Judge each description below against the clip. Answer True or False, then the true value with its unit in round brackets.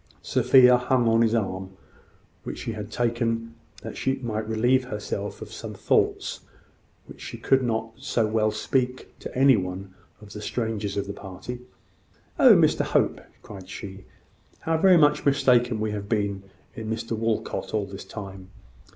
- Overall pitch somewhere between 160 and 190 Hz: False (110 Hz)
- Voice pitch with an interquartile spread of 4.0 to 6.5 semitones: False (3.3 semitones)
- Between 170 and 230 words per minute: False (160 wpm)